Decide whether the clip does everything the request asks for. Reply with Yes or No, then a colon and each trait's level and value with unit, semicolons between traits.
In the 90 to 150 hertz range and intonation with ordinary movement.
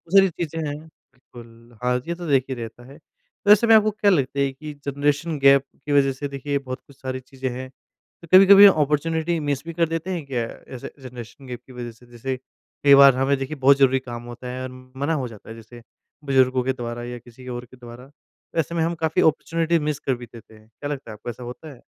Yes: low, 135 Hz; average, 3.7 semitones